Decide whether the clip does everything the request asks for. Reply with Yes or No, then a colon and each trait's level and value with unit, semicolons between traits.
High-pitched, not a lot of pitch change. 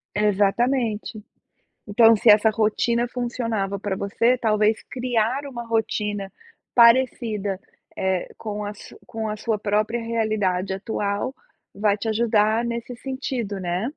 Yes: high, 220 Hz; narrow, 2.3 semitones